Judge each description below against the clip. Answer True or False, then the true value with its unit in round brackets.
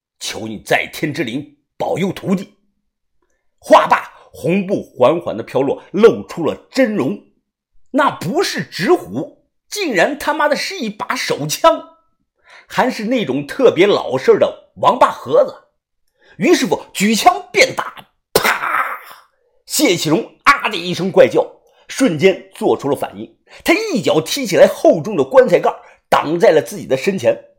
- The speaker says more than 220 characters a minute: False (210 characters per minute)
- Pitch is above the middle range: True (285 Hz)